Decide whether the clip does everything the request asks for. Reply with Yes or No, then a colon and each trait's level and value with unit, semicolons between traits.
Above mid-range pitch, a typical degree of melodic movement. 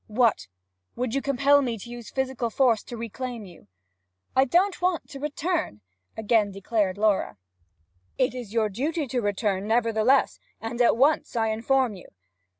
Yes: high, 235 Hz; average, 3.8 semitones